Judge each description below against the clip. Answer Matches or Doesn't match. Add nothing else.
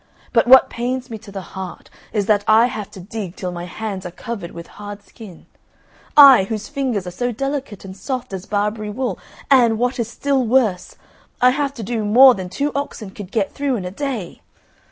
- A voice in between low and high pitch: Doesn't match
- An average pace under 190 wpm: Doesn't match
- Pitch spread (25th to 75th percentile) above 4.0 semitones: Matches